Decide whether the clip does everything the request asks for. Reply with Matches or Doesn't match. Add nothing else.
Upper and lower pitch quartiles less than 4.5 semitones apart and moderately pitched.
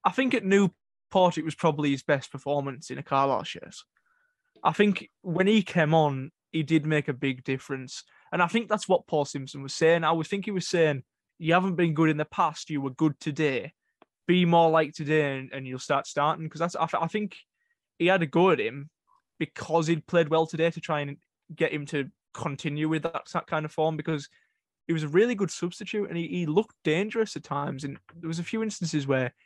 Matches